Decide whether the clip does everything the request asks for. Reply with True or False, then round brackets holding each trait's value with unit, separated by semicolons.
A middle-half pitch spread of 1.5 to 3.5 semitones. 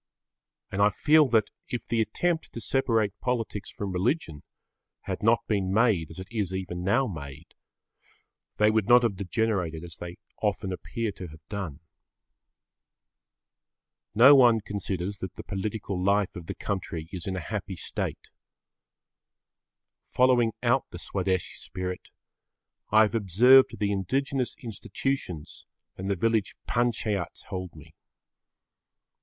False (4.0 semitones)